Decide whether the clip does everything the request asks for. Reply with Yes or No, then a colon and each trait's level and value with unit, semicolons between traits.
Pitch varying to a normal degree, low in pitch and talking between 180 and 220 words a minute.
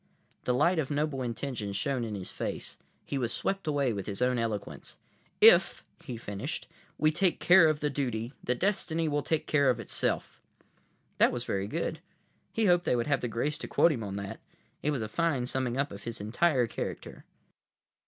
Yes: average, 4.9 semitones; low, 130 Hz; average, 195 wpm